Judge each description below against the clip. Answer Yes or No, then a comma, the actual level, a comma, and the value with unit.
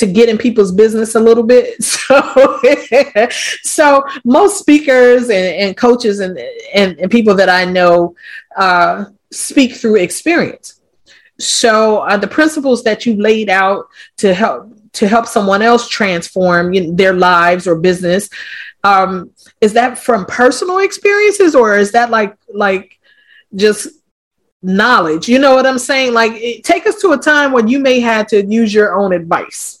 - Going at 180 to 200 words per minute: No, average, 165 wpm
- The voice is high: Yes, high, 225 Hz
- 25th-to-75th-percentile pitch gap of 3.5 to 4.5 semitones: No, average, 4.9 semitones